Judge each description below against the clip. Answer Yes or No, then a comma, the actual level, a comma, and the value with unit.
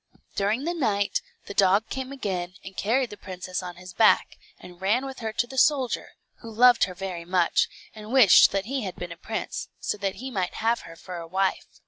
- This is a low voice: No, high, 200 Hz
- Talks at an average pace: No, fast, 215 wpm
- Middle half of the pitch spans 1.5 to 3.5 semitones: No, average, 4.7 semitones